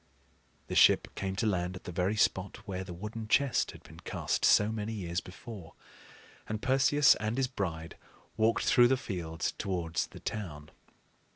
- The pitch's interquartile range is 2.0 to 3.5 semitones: No, average, 4.0 semitones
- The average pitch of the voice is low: Yes, low, 100 Hz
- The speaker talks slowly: No, average, 170 wpm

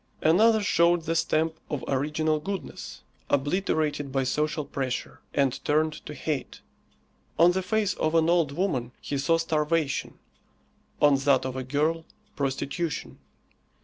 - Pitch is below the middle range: No, medium, 155 Hz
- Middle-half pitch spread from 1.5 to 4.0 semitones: Yes, average, 2.9 semitones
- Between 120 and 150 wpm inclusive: Yes, slow, 135 wpm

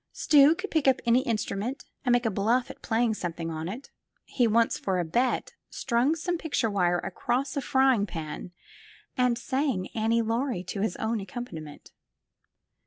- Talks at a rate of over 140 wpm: Yes, average, 170 wpm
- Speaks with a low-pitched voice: No, high, 235 Hz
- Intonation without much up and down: No, average, 5.0 semitones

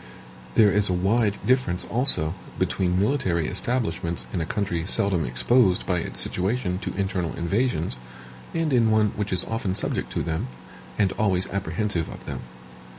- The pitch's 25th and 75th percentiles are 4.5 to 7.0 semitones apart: No, average, 4.0 semitones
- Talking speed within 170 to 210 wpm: No, average, 155 wpm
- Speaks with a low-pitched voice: Yes, very low, 95 Hz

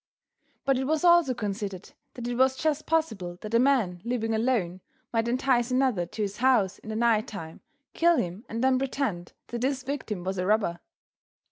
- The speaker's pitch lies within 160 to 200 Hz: No, high, 235 Hz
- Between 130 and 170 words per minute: No, average, 190 wpm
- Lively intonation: No, average, 4.9 semitones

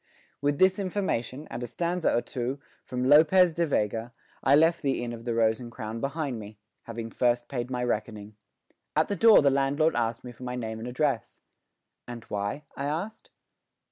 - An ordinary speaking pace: Yes, average, 190 wpm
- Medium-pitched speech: No, low, 125 Hz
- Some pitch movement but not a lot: Yes, average, 4.6 semitones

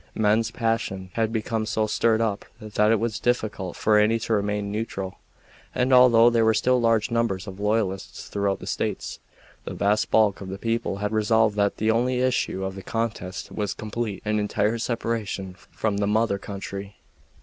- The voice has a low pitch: Yes, low, 110 Hz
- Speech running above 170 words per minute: Yes, average, 180 wpm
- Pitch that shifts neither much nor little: No, narrow, 2.2 semitones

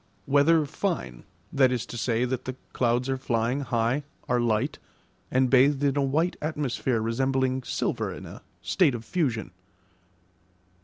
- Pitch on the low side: Yes, low, 130 Hz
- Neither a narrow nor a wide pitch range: Yes, average, 3.1 semitones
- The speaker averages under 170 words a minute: Yes, average, 150 wpm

